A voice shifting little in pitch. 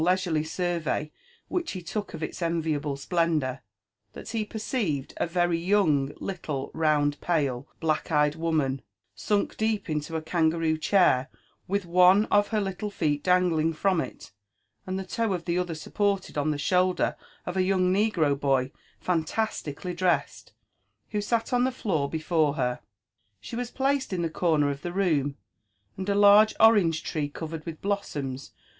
No: average, 4.4 semitones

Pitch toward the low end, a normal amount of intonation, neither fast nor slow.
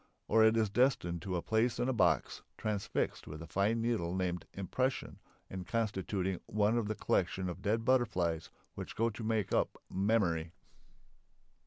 Yes: low, 105 Hz; average, 4.1 semitones; average, 165 wpm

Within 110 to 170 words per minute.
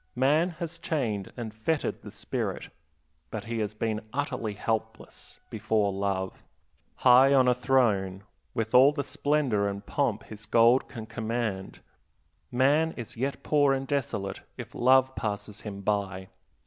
Yes: average, 145 wpm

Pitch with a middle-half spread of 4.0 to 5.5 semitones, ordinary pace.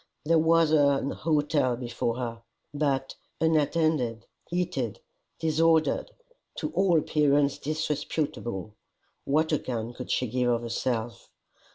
No: average, 4.5 semitones; slow, 105 wpm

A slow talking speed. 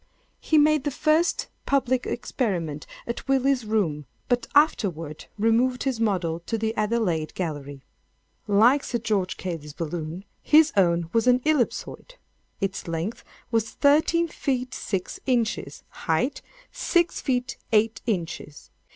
Yes: slow, 125 wpm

